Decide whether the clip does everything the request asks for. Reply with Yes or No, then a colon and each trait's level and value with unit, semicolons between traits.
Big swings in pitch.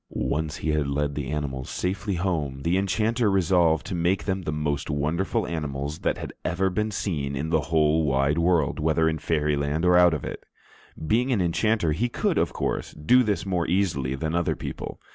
No: average, 4.1 semitones